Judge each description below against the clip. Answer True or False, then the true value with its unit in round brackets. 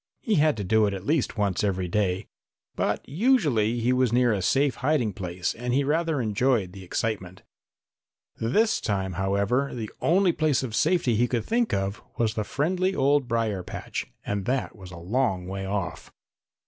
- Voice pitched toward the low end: True (115 Hz)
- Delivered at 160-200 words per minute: True (180 wpm)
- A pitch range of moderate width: False (6.2 semitones)